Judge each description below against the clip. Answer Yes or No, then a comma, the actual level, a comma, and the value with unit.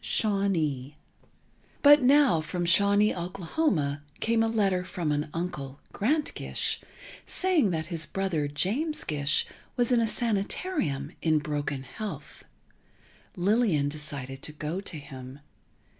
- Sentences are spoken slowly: Yes, slow, 130 wpm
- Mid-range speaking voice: Yes, medium, 175 Hz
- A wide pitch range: Yes, wide, 6.6 semitones